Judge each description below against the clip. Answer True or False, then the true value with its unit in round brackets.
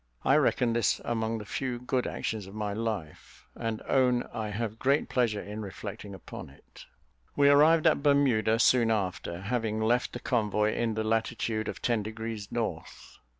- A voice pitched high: False (110 Hz)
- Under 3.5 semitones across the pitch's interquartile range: True (2.4 semitones)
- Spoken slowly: False (170 wpm)